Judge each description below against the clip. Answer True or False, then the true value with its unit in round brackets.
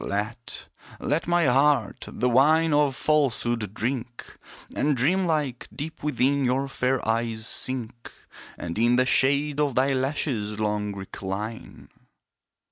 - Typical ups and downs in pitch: True (4.1 semitones)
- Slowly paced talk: True (125 wpm)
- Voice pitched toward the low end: True (130 Hz)